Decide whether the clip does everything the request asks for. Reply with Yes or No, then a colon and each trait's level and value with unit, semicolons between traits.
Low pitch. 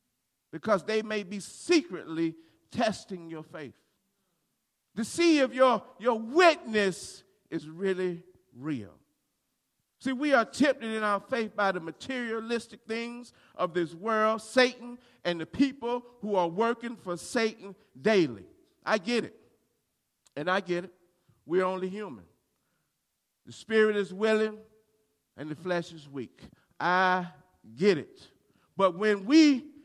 No: high, 210 Hz